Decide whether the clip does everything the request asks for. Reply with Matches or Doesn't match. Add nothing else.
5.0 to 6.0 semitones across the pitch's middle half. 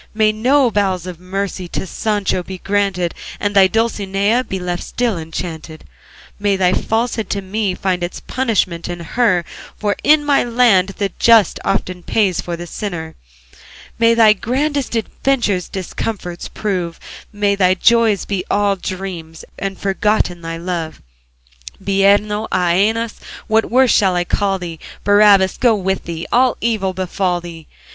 Doesn't match